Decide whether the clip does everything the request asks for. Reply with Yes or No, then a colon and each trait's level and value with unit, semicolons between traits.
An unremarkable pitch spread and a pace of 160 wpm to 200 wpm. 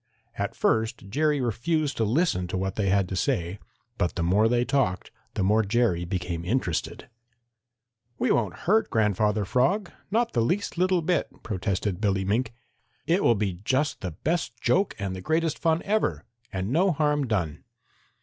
No: wide, 8.3 semitones; average, 170 wpm